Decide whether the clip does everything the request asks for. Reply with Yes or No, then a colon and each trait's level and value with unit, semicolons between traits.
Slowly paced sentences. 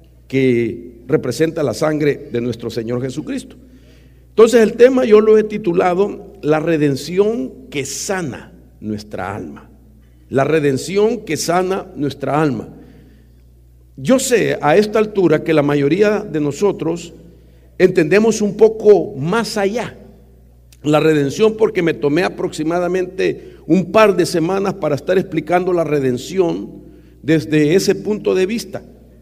Yes: slow, 125 wpm